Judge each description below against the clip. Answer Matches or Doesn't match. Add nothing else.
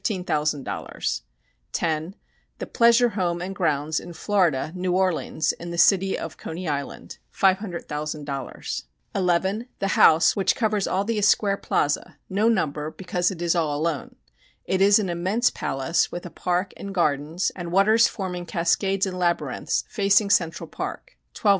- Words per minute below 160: Matches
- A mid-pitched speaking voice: Matches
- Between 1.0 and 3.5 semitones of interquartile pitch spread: Matches